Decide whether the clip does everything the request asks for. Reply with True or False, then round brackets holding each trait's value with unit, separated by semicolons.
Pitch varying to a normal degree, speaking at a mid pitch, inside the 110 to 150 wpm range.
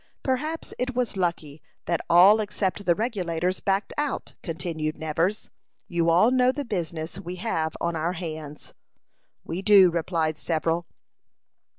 True (4.3 semitones; 175 Hz; 135 wpm)